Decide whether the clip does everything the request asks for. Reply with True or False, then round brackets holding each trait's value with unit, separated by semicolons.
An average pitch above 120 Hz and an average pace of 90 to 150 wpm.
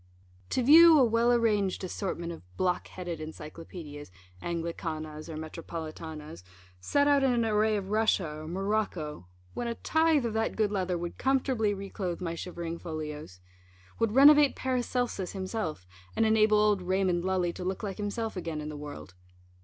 False (190 Hz; 160 wpm)